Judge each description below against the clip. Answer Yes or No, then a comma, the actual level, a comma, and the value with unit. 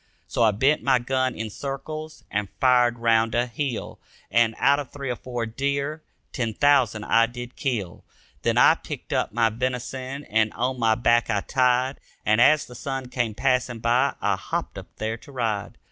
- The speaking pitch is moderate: No, low, 125 Hz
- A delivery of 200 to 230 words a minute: No, average, 185 wpm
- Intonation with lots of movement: No, average, 2.8 semitones